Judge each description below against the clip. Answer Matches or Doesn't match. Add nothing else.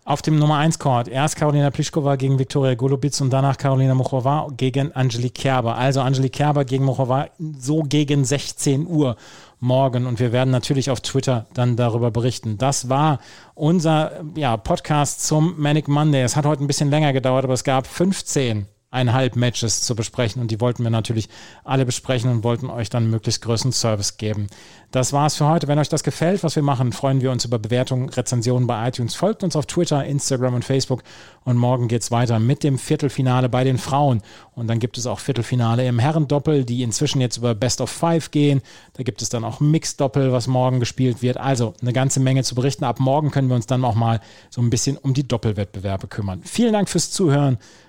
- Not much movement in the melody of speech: Doesn't match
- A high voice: Doesn't match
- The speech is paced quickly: Matches